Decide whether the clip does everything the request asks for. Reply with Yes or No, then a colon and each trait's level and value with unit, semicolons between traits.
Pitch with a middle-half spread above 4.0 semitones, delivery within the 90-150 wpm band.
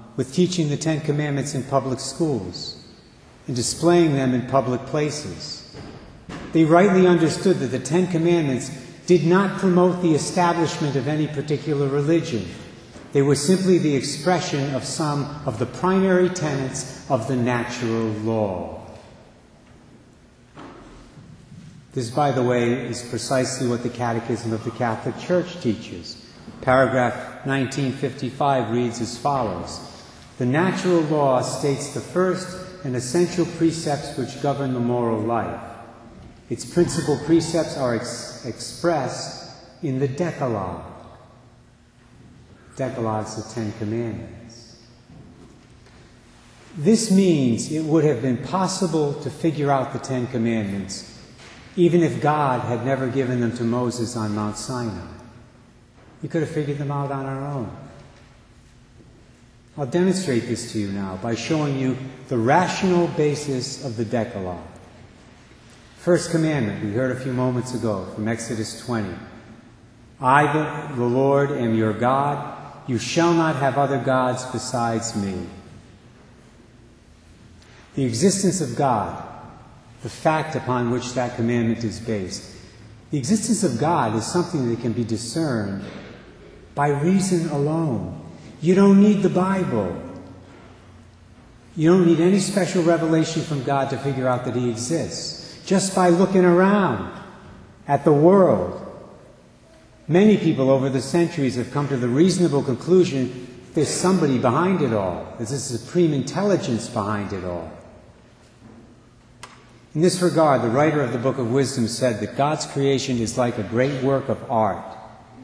Yes: average, 5.2 semitones; slow, 135 wpm